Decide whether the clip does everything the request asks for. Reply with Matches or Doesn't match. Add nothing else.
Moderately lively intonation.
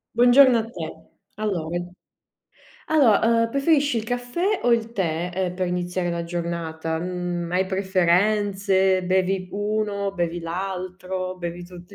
Matches